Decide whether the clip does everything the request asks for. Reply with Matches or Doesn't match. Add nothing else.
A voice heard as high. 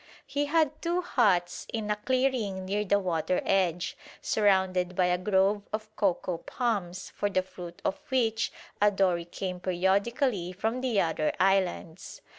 Matches